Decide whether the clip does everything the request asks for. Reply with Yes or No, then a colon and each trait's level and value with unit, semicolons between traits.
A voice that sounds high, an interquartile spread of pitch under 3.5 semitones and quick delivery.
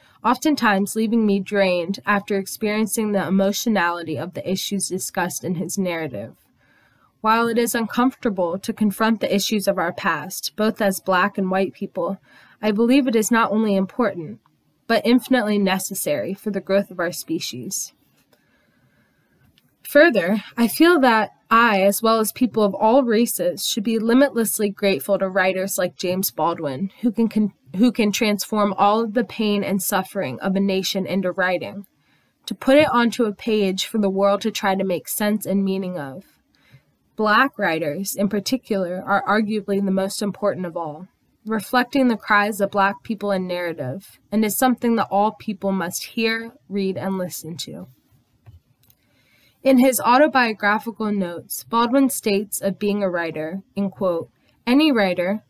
No: high, 200 Hz; average, 3.1 semitones; average, 160 wpm